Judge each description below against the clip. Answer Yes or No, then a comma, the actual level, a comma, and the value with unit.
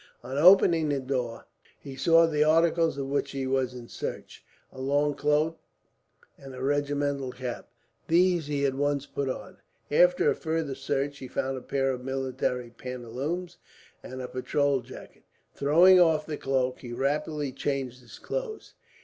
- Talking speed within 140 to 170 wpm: Yes, average, 160 wpm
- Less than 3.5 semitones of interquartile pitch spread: Yes, average, 2.9 semitones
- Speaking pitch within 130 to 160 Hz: Yes, medium, 140 Hz